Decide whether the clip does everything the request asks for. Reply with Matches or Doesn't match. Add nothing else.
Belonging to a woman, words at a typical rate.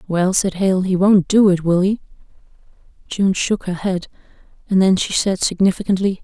Matches